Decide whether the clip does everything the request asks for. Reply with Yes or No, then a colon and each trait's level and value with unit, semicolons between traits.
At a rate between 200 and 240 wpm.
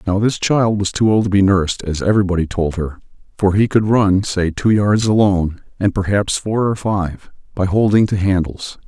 Yes: fast, 205 wpm